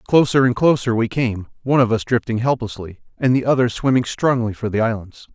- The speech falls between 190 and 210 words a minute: Yes, average, 200 wpm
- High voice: No, low, 120 Hz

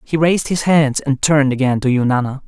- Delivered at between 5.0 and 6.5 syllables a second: Yes, 5.9 syllables/s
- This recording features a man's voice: Yes, male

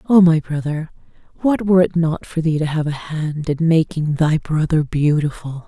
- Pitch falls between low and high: Yes, medium, 160 Hz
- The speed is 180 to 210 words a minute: Yes, average, 190 wpm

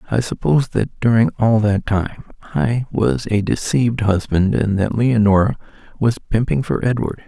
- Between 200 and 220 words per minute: No, average, 155 wpm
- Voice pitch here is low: Yes, low, 110 Hz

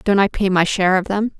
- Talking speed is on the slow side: No, fast, 300 wpm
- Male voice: No, female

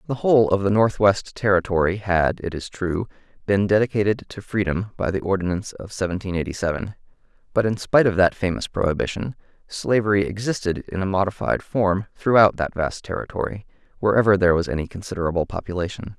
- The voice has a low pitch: Yes, very low, 95 Hz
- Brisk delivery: No, average, 165 wpm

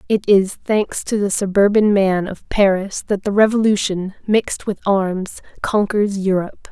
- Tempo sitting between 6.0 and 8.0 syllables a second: No, 4.4 syllables/s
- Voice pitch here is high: Yes, high, 200 Hz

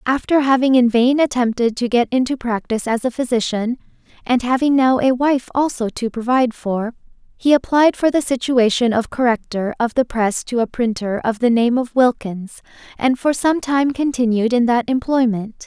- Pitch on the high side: Yes, high, 245 Hz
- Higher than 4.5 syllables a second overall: Yes, 5.1 syllables/s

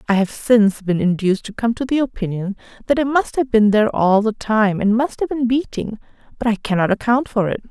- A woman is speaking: Yes, female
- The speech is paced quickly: Yes, fast, 235 wpm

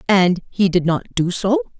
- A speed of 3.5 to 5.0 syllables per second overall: Yes, 4.6 syllables/s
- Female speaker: Yes, female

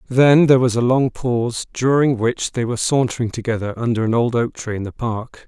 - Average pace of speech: No, fast, 220 wpm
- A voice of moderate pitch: No, low, 120 Hz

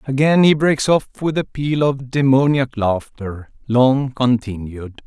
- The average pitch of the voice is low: Yes, low, 130 Hz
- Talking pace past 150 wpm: No, average, 140 wpm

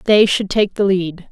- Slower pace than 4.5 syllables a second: Yes, 4.3 syllables/s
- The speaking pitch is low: No, high, 195 Hz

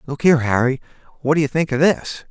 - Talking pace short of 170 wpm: No, fast, 210 wpm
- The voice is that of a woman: No, male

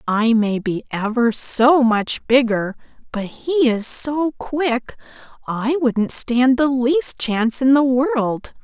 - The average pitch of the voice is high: Yes, very high, 250 Hz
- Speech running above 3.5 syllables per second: No, 3.2 syllables/s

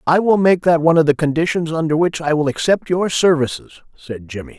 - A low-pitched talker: No, medium, 160 Hz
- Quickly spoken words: Yes, fast, 225 wpm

